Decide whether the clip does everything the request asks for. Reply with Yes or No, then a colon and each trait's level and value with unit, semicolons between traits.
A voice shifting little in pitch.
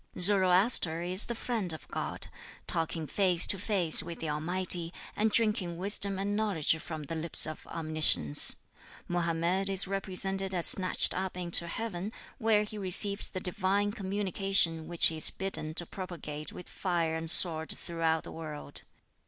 No: average, 3.1 semitones